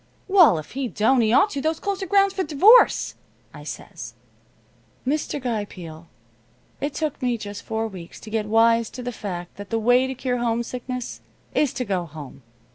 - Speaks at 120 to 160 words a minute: No, average, 190 wpm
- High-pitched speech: Yes, high, 240 Hz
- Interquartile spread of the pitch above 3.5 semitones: Yes, average, 5.0 semitones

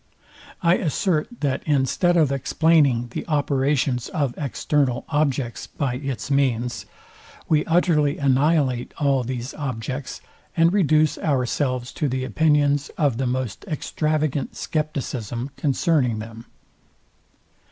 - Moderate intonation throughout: Yes, average, 3.2 semitones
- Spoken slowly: Yes, slow, 110 wpm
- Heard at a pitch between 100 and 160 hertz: Yes, medium, 140 Hz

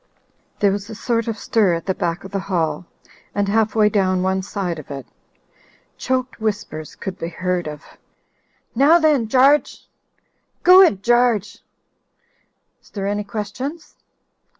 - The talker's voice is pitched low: No, high, 205 Hz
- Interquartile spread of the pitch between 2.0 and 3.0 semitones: No, average, 4.0 semitones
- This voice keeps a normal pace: Yes, average, 150 wpm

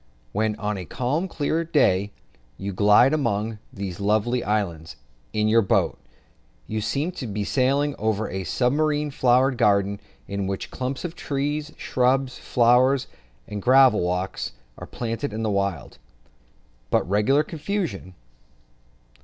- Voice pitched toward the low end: Yes, low, 115 Hz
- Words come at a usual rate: No, slow, 130 wpm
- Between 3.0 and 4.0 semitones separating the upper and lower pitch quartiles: No, average, 5.3 semitones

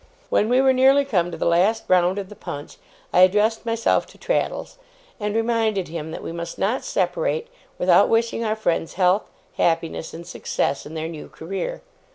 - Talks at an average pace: Yes, average, 185 wpm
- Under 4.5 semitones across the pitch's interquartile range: No, average, 5.2 semitones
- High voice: Yes, high, 200 Hz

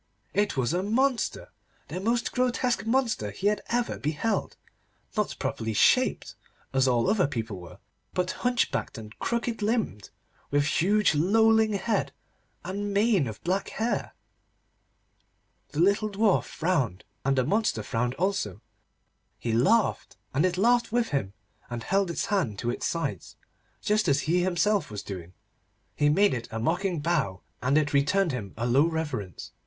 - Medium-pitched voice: Yes, medium, 175 Hz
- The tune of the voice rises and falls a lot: Yes, wide, 8.8 semitones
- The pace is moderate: Yes, average, 155 wpm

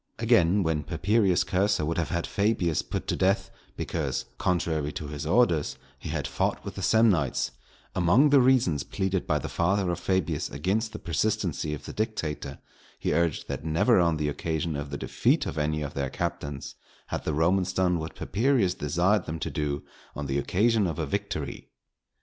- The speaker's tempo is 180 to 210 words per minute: Yes, average, 185 wpm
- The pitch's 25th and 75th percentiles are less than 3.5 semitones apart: No, average, 4.7 semitones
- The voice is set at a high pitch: No, very low, 85 Hz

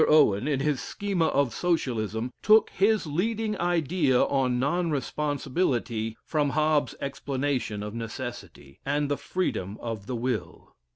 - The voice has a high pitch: No, medium, 140 Hz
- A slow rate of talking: Yes, slow, 130 wpm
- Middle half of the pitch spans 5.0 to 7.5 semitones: Yes, wide, 5.4 semitones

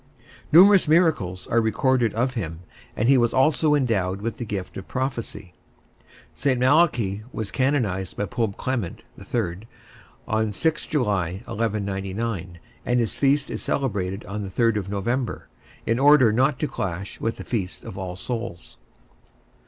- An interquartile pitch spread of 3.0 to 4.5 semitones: No, average, 5.0 semitones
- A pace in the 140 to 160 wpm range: Yes, average, 145 wpm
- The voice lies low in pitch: Yes, low, 115 Hz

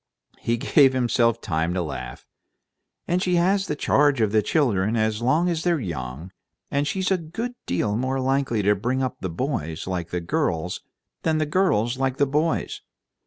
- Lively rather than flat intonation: Yes, wide, 7.9 semitones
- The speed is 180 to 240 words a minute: No, average, 170 wpm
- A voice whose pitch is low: Yes, low, 125 Hz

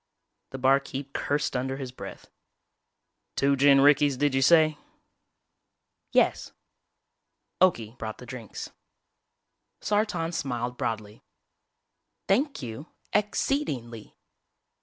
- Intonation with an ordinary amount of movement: Yes, average, 4.1 semitones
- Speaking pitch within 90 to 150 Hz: Yes, low, 135 Hz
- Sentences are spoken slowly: Yes, slow, 105 wpm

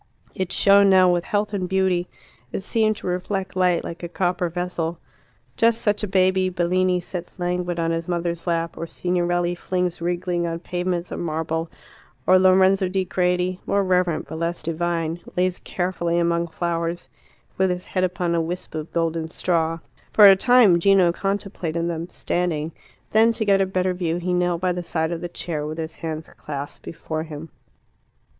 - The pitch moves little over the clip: Yes, narrow, 1.7 semitones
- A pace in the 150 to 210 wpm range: Yes, average, 175 wpm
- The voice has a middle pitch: Yes, medium, 175 Hz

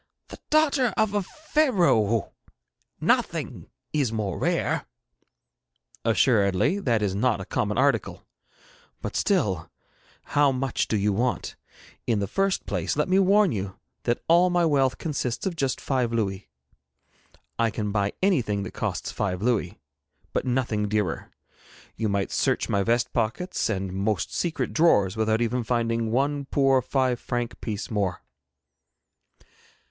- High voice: No, low, 120 Hz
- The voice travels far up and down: Yes, wide, 5.9 semitones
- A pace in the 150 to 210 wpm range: No, average, 140 wpm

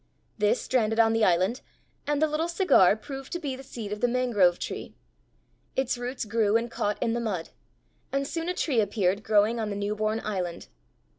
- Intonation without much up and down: No, average, 4.0 semitones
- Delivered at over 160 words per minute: Yes, average, 200 wpm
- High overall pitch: Yes, high, 225 Hz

